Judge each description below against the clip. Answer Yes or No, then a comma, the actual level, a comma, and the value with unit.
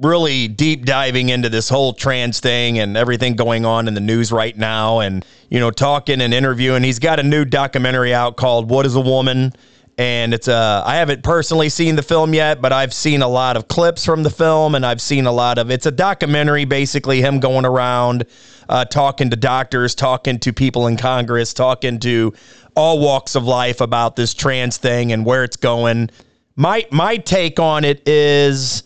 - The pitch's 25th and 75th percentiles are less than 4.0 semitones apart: Yes, average, 2.9 semitones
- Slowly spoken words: No, average, 200 wpm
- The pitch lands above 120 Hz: Yes, low, 130 Hz